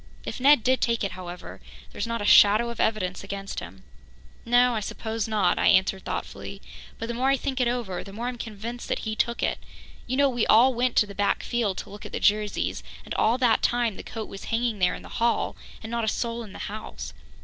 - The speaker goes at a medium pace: No, fast, 235 wpm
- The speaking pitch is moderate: No, high, 225 Hz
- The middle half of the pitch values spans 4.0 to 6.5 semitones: No, average, 3.0 semitones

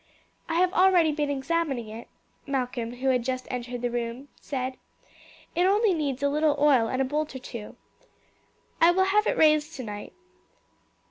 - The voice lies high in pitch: Yes, very high, 275 Hz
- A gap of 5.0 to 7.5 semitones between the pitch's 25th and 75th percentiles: No, average, 4.6 semitones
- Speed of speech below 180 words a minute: Yes, average, 170 wpm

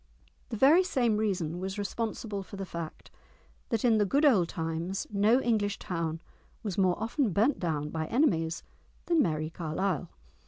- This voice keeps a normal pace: Yes, average, 160 wpm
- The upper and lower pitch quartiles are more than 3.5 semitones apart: Yes, average, 5.3 semitones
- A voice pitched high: Yes, high, 195 Hz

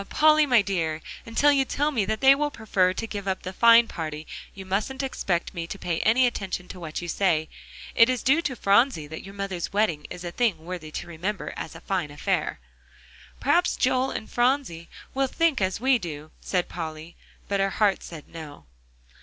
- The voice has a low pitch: No, high, 195 Hz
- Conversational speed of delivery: Yes, average, 195 wpm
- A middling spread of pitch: No, wide, 6.8 semitones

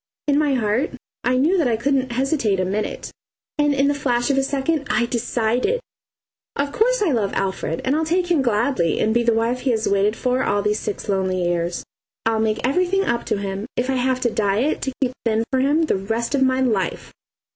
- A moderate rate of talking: No, fast, 220 wpm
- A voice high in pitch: Yes, high, 245 Hz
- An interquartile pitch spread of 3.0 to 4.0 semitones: No, average, 4.6 semitones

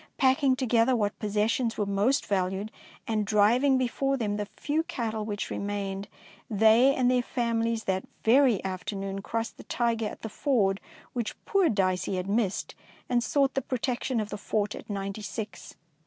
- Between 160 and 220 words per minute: Yes, average, 170 wpm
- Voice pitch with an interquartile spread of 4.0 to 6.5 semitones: No, average, 3.6 semitones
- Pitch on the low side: No, high, 220 Hz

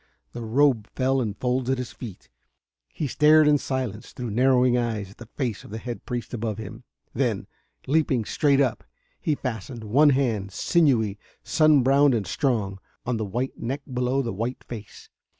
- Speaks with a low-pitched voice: Yes, low, 125 Hz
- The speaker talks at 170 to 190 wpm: Yes, average, 175 wpm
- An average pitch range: Yes, average, 3.5 semitones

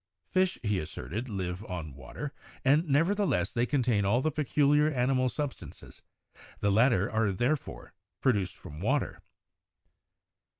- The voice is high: No, low, 120 Hz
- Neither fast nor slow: No, slow, 130 wpm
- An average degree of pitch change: No, wide, 7.0 semitones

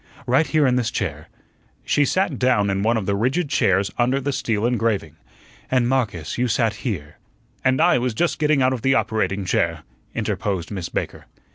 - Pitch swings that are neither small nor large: Yes, average, 4.7 semitones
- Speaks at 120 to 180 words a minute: No, average, 190 wpm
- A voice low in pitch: Yes, low, 115 Hz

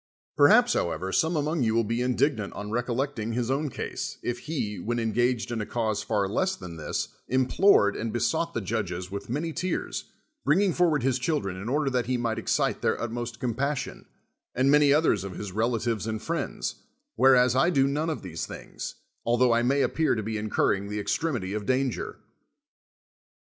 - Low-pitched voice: Yes, low, 120 Hz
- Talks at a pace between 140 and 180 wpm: No, average, 190 wpm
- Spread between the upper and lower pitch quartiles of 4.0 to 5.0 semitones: Yes, average, 4.4 semitones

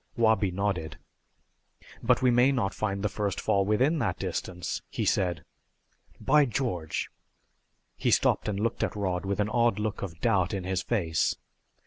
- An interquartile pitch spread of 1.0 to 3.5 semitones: No, average, 4.0 semitones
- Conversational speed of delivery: Yes, average, 165 wpm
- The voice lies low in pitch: Yes, low, 100 Hz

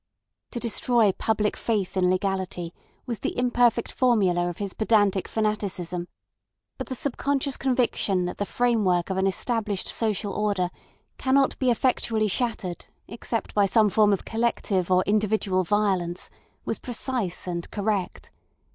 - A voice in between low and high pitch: No, high, 210 Hz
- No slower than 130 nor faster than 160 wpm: Yes, average, 140 wpm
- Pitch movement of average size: Yes, average, 4.0 semitones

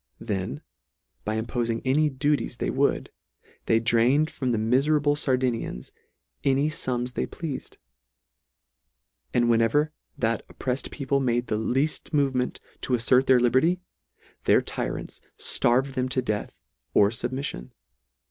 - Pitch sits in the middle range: No, low, 125 Hz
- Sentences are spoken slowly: Yes, slow, 130 wpm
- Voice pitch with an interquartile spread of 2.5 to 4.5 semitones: Yes, average, 3.1 semitones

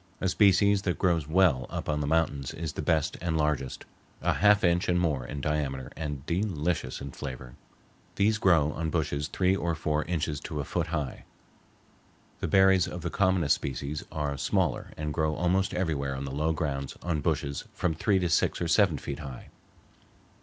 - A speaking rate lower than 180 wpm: No, average, 185 wpm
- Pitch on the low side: Yes, very low, 80 Hz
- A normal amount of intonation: Yes, average, 3.7 semitones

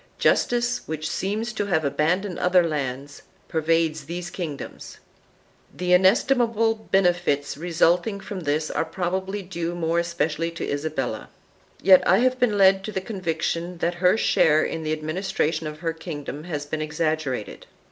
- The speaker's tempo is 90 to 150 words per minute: Yes, average, 145 wpm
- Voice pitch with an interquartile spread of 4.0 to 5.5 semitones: No, average, 3.5 semitones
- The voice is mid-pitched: Yes, medium, 170 Hz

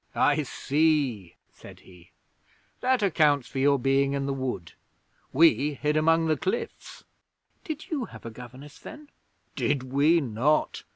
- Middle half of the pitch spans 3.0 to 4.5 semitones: Yes, average, 3.7 semitones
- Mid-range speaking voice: Yes, medium, 145 Hz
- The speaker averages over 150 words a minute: No, average, 140 wpm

